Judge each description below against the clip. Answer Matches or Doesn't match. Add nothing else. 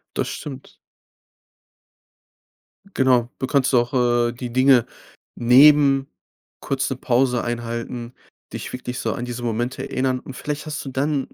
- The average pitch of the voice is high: Doesn't match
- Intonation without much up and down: Matches